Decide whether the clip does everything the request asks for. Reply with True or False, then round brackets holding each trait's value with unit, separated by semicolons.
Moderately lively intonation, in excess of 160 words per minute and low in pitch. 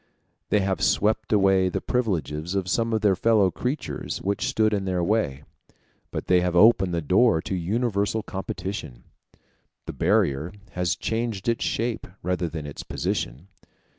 False (4.0 semitones; 155 wpm; 95 Hz)